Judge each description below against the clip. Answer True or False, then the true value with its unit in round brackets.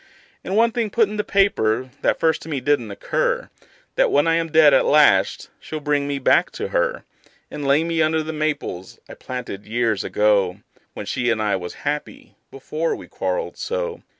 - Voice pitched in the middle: True (150 Hz)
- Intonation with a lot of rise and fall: True (5.8 semitones)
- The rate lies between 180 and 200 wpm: True (195 wpm)